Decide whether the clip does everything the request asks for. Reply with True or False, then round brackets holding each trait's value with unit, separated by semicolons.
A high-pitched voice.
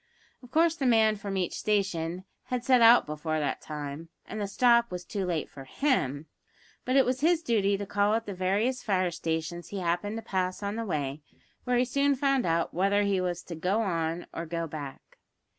True (195 Hz)